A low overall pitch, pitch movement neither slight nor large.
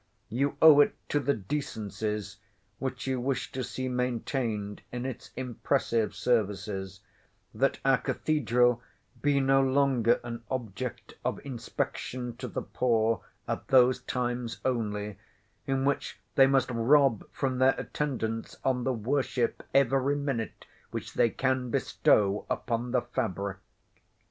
Yes: low, 125 Hz; average, 3.0 semitones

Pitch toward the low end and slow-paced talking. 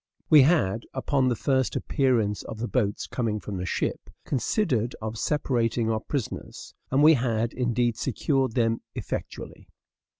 No: low, 120 Hz; average, 145 wpm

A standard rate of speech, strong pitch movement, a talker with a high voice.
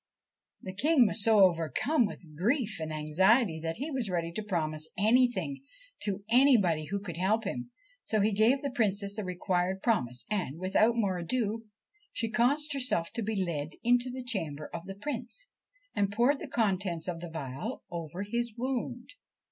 Yes: average, 170 wpm; wide, 5.8 semitones; high, 205 Hz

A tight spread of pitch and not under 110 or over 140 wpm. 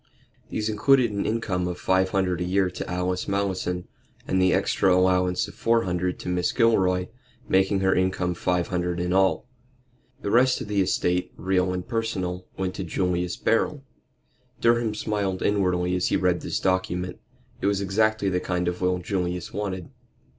No: narrow, 2.0 semitones; average, 170 wpm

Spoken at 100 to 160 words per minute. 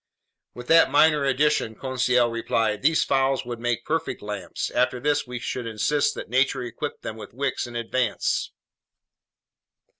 Yes: average, 150 wpm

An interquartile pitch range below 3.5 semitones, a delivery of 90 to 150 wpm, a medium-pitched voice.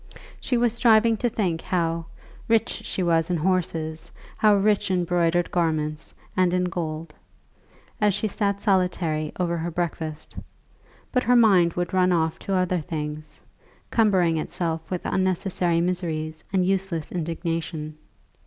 Yes: average, 2.8 semitones; average, 140 wpm; medium, 175 Hz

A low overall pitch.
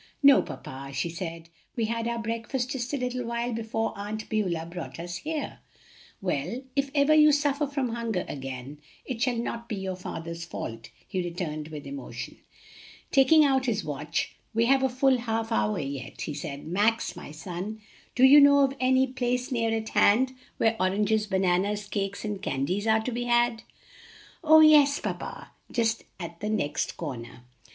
No: high, 220 Hz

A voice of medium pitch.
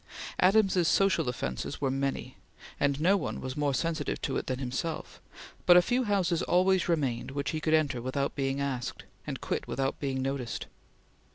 Yes: medium, 145 Hz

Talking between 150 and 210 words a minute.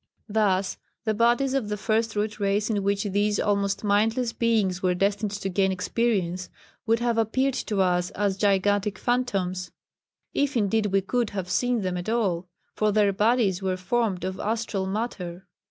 Yes: average, 170 wpm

